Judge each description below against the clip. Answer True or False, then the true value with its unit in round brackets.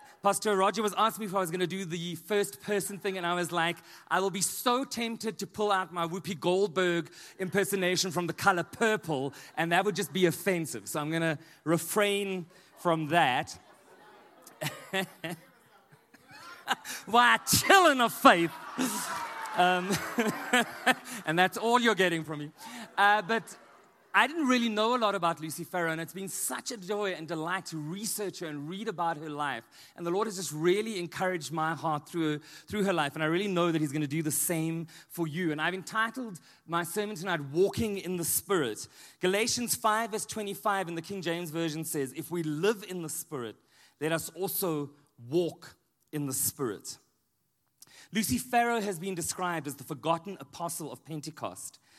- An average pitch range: True (4.1 semitones)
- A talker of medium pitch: True (180 Hz)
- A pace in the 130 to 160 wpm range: False (180 wpm)